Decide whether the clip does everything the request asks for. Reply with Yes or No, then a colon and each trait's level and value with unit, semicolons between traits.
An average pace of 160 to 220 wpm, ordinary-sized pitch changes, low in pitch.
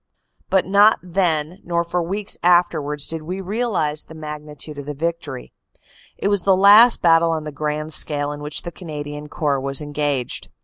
No: average, 175 wpm; average, 3.3 semitones; medium, 160 Hz